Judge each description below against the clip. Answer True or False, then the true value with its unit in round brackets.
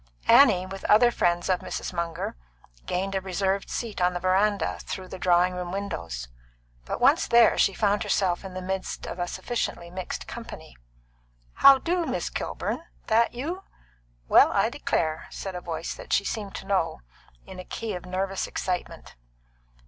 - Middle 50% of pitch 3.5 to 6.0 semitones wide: False (2.7 semitones)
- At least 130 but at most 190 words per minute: True (170 wpm)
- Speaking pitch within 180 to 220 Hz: True (190 Hz)